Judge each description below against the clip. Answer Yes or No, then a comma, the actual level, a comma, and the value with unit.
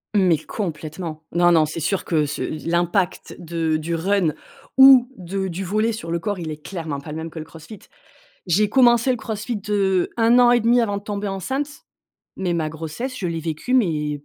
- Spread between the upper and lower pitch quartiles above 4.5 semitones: Yes, average, 4.9 semitones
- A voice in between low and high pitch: Yes, medium, 180 Hz